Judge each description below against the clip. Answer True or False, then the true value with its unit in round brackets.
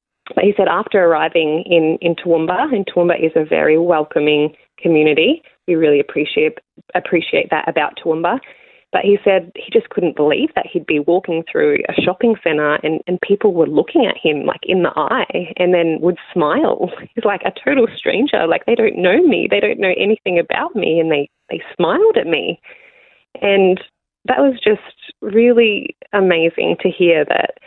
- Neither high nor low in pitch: True (180 Hz)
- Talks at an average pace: True (180 wpm)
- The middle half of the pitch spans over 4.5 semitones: True (5.1 semitones)